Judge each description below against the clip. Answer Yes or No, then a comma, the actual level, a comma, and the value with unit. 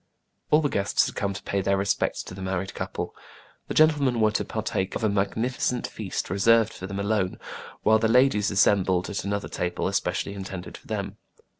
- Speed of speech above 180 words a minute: Yes, average, 190 wpm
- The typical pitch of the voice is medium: No, low, 100 Hz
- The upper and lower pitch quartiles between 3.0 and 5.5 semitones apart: No, narrow, 2.6 semitones